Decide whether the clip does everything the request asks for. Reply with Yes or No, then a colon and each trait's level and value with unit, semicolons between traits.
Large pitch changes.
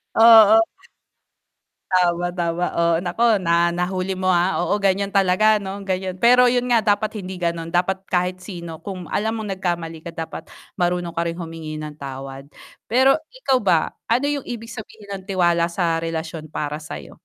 No: average, 3.4 semitones